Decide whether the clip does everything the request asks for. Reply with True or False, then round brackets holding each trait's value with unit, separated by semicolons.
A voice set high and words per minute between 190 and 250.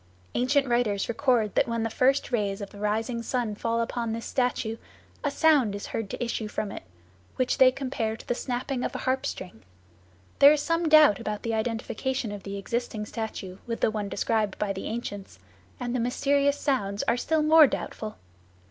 True (230 Hz; 195 wpm)